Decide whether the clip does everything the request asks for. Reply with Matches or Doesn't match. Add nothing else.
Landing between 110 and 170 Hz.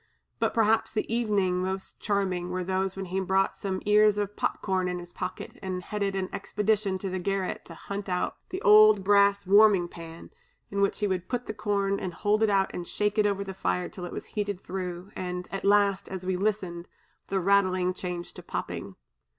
Doesn't match